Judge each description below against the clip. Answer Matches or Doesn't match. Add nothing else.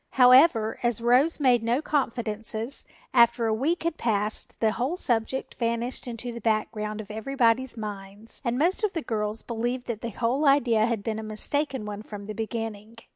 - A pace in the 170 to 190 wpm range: Matches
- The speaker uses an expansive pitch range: Doesn't match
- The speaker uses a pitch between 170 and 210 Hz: Doesn't match